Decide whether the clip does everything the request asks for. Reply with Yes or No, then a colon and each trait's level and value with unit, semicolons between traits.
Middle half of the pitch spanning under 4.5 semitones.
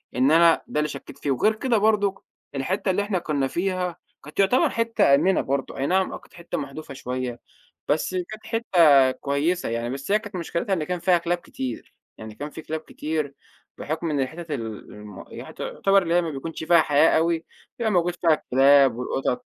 No: average, 4.9 semitones